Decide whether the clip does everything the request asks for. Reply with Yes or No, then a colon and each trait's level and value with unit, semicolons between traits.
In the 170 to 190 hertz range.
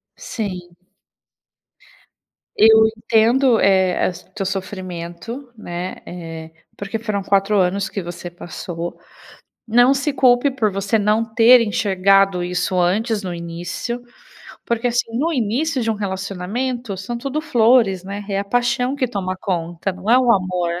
No: high, 200 Hz